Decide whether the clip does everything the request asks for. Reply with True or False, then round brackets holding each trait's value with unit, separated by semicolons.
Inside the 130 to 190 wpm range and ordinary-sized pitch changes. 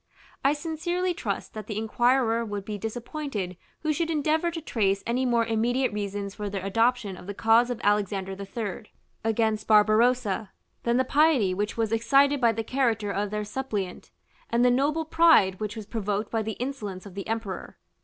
True (180 wpm; 4.1 semitones)